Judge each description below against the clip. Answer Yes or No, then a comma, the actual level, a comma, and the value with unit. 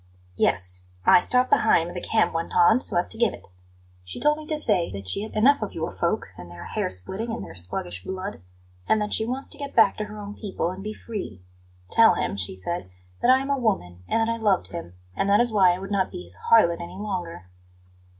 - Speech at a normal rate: No, fast, 245 wpm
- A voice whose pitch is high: Yes, high, 195 Hz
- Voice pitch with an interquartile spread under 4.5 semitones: No, wide, 5.4 semitones